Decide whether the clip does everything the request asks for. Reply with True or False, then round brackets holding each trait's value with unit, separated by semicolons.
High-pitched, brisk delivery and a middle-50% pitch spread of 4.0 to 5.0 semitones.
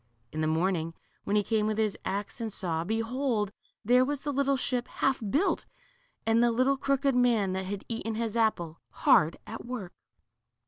False (225 Hz; 180 wpm; 4.5 semitones)